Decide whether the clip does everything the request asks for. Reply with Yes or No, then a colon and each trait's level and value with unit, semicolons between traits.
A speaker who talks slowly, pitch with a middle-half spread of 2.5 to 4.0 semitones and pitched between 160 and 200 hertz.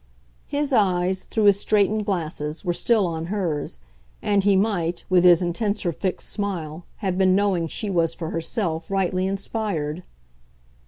No: average, 150 wpm; average, 3.3 semitones; medium, 185 Hz